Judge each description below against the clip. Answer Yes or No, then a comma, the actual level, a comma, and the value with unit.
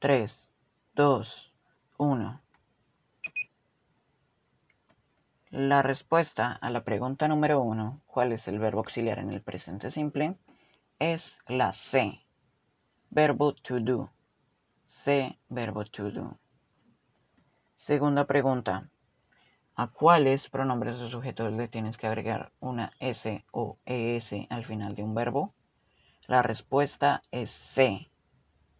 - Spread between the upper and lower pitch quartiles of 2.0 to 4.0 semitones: No, average, 4.4 semitones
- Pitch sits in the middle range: No, low, 125 Hz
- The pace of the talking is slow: Yes, slow, 110 wpm